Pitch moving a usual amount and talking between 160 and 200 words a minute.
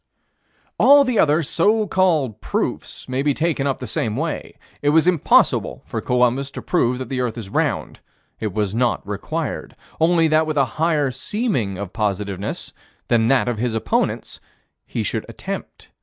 No: wide, 6.2 semitones; average, 170 wpm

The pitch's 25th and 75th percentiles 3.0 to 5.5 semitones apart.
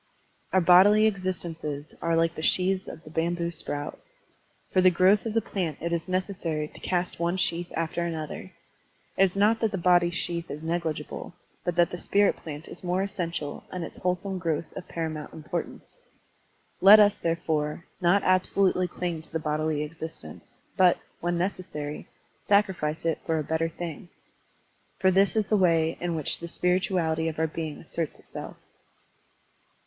No: narrow, 2.6 semitones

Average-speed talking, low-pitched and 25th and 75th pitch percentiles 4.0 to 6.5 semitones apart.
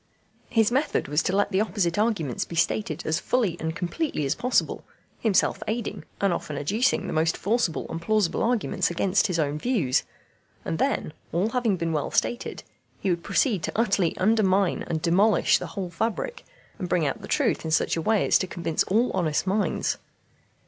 No: average, 185 wpm; high, 190 Hz; average, 4.9 semitones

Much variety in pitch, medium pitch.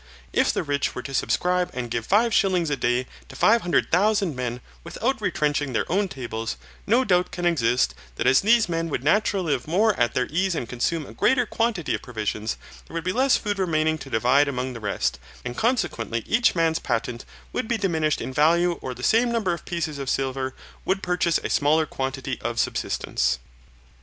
Yes: wide, 6.7 semitones; medium, 155 Hz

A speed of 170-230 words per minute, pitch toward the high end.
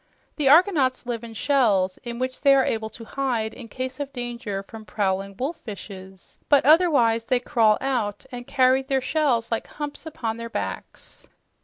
Yes: average, 175 wpm; high, 245 Hz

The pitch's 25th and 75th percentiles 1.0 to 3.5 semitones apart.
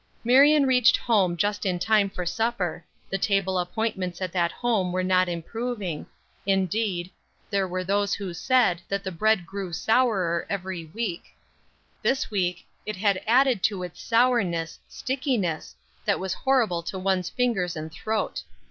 No: average, 3.9 semitones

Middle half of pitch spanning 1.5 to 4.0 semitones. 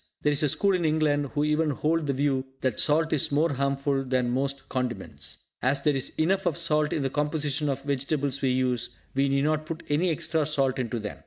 Yes: narrow, 2.4 semitones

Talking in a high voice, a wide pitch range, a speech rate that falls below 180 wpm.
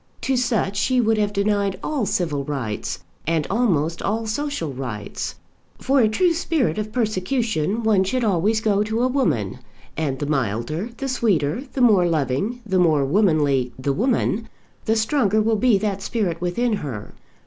Yes: high, 200 Hz; wide, 6.9 semitones; average, 165 wpm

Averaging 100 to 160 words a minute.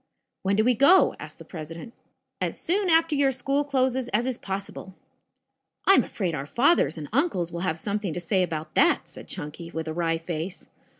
No: average, 195 wpm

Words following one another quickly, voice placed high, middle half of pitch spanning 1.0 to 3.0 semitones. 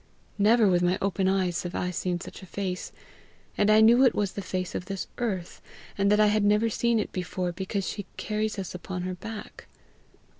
Yes: fast, 210 wpm; high, 195 Hz; narrow, 2.6 semitones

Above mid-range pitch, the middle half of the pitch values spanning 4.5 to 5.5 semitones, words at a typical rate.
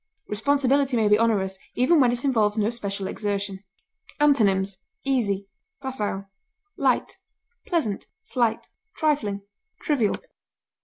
No: high, 220 Hz; average, 4.8 semitones; slow, 105 wpm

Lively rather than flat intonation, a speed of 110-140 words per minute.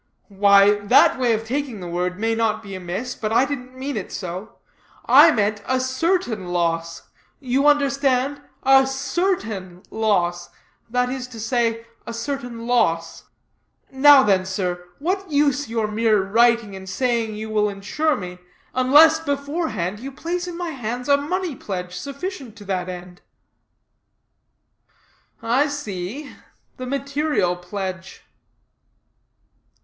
Yes: wide, 6.1 semitones; slow, 135 wpm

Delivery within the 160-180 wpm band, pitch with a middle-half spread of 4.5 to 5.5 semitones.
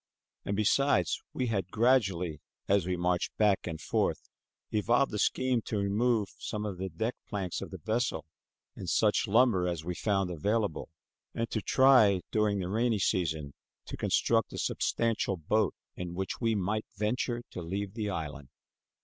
No: average, 165 wpm; average, 4.0 semitones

